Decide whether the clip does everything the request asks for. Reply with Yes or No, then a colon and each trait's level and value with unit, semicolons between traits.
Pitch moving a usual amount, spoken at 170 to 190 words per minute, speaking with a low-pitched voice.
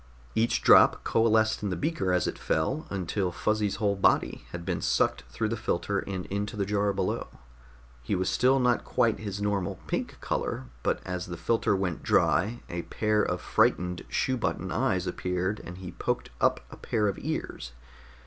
Yes: average, 3.0 semitones; average, 180 wpm; low, 100 Hz